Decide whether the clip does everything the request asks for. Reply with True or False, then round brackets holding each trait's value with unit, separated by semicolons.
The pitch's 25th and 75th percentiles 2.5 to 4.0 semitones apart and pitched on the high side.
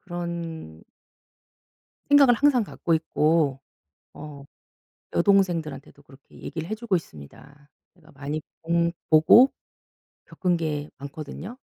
False (3.7 semitones; 160 Hz)